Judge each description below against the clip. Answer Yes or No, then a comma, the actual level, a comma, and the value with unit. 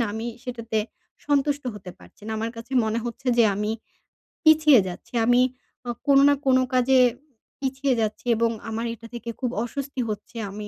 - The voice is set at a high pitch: Yes, high, 240 Hz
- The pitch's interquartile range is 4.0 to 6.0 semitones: No, average, 3.4 semitones